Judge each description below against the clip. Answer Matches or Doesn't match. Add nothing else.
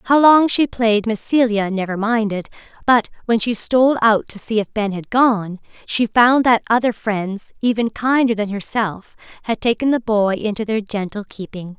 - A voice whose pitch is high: Matches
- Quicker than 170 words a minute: Matches